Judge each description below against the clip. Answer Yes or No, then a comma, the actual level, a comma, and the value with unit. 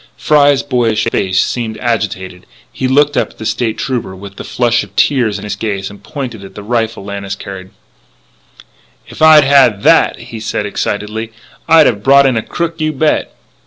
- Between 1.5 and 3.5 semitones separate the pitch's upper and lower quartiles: No, average, 5.0 semitones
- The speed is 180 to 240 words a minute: Yes, average, 185 wpm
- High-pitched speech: No, low, 115 Hz